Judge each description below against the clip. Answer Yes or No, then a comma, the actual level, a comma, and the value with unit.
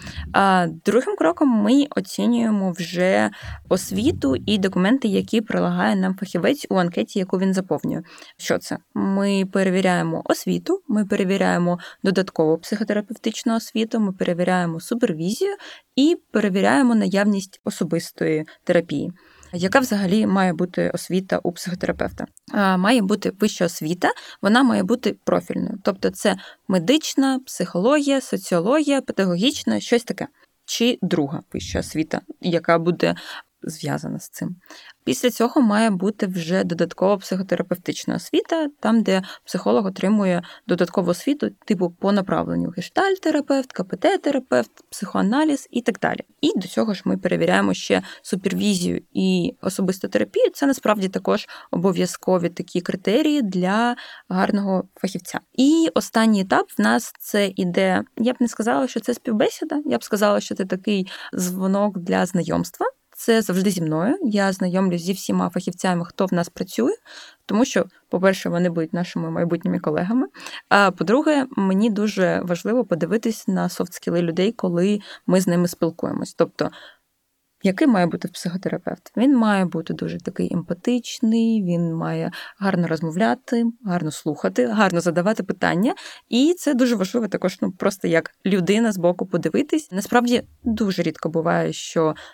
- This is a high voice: Yes, high, 195 Hz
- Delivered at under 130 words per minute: No, average, 135 wpm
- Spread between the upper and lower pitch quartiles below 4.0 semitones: No, average, 5.1 semitones